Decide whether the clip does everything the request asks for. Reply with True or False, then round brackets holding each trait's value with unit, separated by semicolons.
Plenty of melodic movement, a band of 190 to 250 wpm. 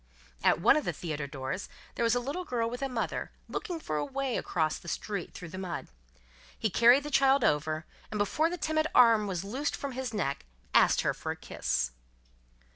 True (8.2 semitones; 205 wpm)